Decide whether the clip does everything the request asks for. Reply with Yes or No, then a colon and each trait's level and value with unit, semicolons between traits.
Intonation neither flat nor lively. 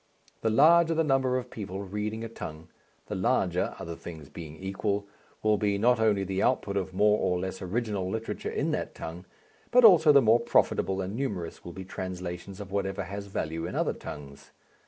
Yes: average, 3.5 semitones